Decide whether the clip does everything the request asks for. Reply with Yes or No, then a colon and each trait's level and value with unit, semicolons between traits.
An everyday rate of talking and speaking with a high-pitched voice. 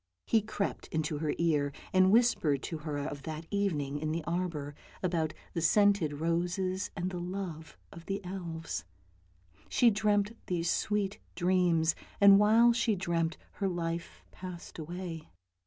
No: average, 145 wpm; medium, 175 Hz